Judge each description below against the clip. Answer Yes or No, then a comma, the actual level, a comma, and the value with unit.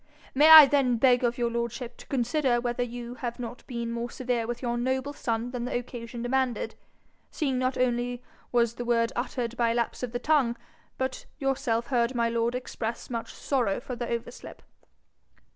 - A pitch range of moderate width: No, narrow, 1.5 semitones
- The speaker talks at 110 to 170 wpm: No, average, 185 wpm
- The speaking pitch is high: Yes, high, 240 Hz